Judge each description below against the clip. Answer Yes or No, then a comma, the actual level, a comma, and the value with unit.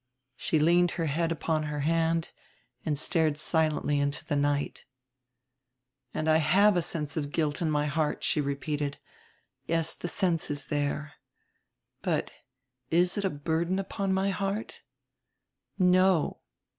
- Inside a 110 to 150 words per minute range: Yes, slow, 135 wpm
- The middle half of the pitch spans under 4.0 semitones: Yes, average, 3.0 semitones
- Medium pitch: Yes, medium, 160 Hz